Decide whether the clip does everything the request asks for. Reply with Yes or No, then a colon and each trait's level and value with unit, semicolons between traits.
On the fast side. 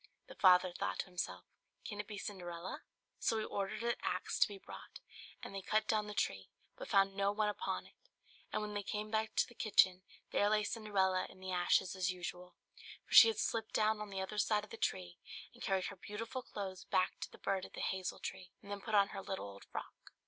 Yes: fast, 230 wpm